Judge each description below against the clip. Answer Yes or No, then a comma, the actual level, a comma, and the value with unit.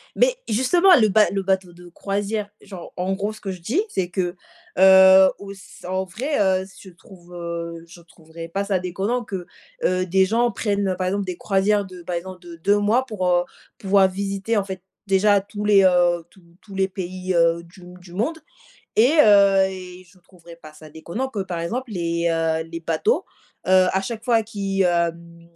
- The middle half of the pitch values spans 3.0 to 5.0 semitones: No, narrow, 2.6 semitones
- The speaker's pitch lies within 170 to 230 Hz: Yes, high, 190 Hz